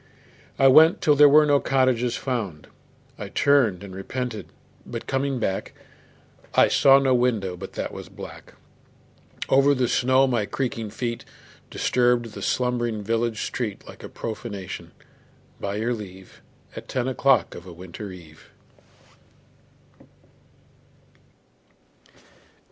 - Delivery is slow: Yes, slow, 120 wpm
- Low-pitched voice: Yes, low, 120 Hz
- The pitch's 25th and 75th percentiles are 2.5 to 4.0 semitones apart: No, average, 4.5 semitones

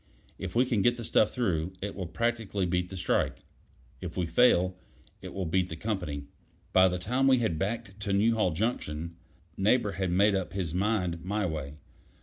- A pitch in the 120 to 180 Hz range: No, very low, 95 Hz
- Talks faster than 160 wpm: Yes, average, 185 wpm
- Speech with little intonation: No, average, 3.6 semitones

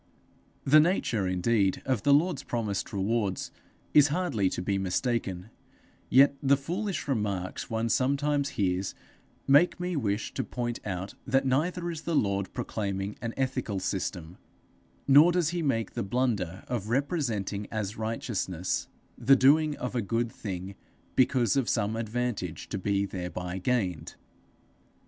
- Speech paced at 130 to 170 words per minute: Yes, average, 140 wpm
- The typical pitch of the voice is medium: No, low, 115 Hz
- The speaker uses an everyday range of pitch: No, wide, 6.0 semitones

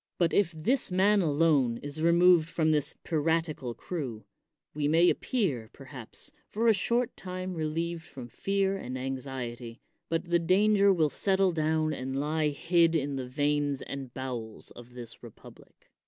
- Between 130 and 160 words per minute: Yes, average, 155 wpm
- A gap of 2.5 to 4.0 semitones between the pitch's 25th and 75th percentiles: No, average, 5.0 semitones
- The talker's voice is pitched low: No, medium, 155 Hz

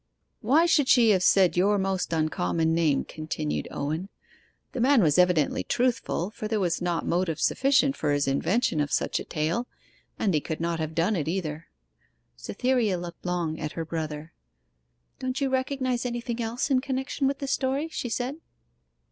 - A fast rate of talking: No, average, 175 wpm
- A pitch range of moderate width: No, wide, 7.9 semitones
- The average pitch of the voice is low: No, medium, 185 Hz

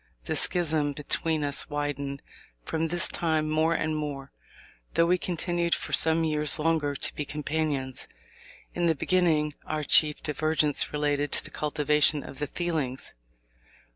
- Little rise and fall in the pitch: Yes, narrow, 1.8 semitones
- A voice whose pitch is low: No, medium, 150 Hz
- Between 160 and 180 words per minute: No, average, 145 wpm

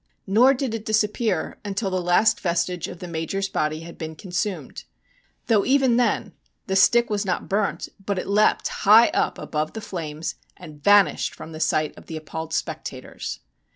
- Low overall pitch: No, high, 190 Hz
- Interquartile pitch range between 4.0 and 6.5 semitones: Yes, average, 4.7 semitones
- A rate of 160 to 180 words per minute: Yes, average, 175 wpm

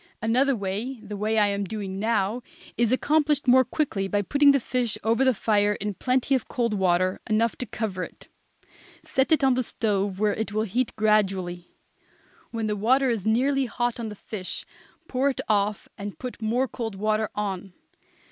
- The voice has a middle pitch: No, high, 220 Hz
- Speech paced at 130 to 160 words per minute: No, average, 185 wpm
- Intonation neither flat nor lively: Yes, average, 3.7 semitones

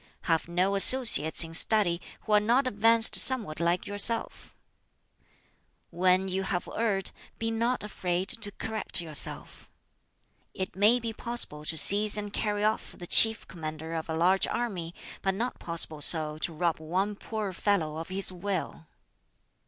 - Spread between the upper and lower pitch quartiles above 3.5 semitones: Yes, average, 4.4 semitones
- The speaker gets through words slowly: No, average, 150 wpm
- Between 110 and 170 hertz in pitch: No, high, 190 Hz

